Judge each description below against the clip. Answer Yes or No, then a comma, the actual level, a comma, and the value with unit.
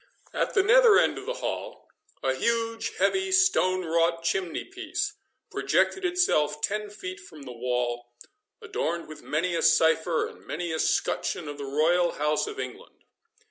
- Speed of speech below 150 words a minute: No, average, 160 wpm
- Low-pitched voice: No, medium, 175 Hz